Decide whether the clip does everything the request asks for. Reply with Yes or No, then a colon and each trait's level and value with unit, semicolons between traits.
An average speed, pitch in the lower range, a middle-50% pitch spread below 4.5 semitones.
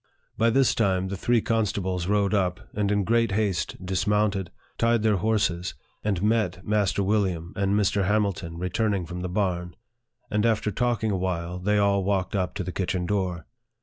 Yes: average, 175 wpm; low, 100 Hz; narrow, 2.6 semitones